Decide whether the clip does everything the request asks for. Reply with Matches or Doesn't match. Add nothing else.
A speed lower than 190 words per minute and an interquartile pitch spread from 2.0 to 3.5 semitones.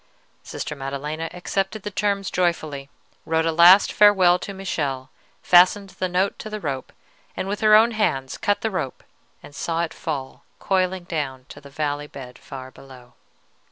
Doesn't match